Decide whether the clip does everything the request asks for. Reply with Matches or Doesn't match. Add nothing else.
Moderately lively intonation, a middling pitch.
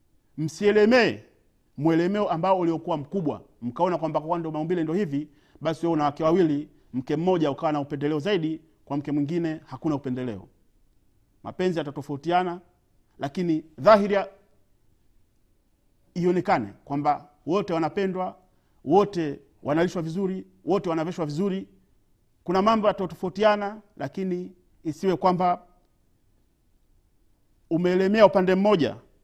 Matches